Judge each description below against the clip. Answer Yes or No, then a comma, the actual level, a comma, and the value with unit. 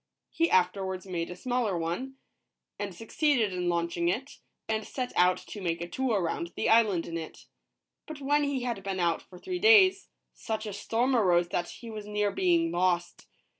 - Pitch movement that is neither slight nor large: No, wide, 6.4 semitones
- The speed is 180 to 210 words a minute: Yes, average, 185 wpm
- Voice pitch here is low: No, high, 205 Hz